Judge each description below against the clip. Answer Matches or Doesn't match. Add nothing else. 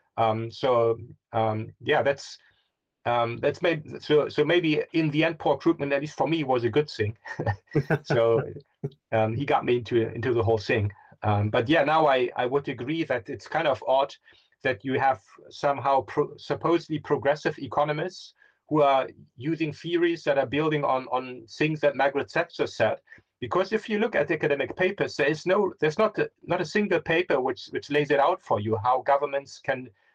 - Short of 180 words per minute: Doesn't match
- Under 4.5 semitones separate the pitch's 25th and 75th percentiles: Matches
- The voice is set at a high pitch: Doesn't match